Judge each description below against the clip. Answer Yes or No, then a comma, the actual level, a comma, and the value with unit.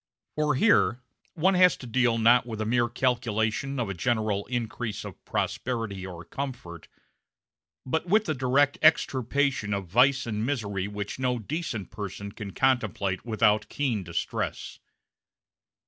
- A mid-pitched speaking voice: No, low, 120 Hz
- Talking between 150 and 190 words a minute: No, average, 140 wpm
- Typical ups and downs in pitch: Yes, average, 4.3 semitones